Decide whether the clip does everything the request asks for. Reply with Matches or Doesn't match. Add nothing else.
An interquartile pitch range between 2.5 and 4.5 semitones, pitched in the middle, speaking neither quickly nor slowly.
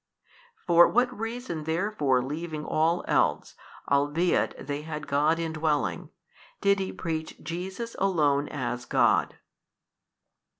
Doesn't match